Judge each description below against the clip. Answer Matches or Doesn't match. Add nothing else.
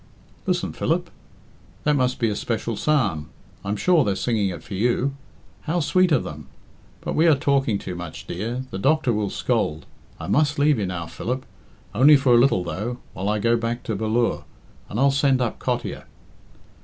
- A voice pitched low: Matches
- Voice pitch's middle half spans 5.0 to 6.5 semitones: Matches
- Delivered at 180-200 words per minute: Matches